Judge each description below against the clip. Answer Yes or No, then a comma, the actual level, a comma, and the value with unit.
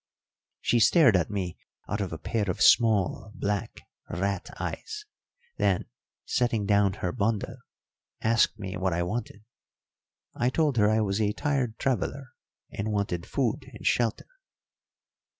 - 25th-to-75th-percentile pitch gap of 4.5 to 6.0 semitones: No, average, 3.3 semitones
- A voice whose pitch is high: No, low, 105 Hz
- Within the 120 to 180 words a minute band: Yes, average, 140 wpm